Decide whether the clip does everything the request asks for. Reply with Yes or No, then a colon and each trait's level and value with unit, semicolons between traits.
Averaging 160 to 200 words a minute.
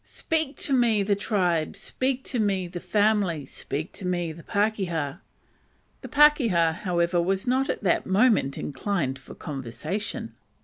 No: average, 145 wpm